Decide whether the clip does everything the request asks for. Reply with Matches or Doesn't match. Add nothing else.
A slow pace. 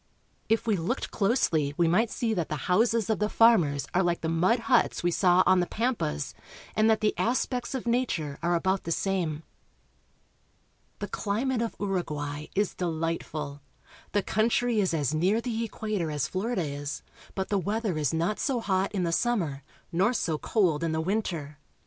Doesn't match